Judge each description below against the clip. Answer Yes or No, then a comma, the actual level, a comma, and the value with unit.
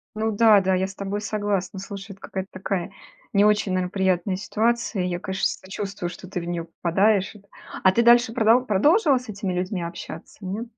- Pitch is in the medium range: No, high, 195 Hz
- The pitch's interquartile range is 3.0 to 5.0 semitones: No, narrow, 2.6 semitones